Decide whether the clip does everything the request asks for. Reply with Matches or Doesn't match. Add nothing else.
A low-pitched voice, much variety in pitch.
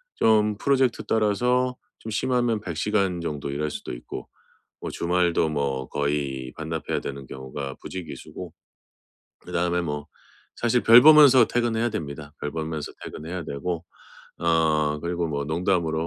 Matches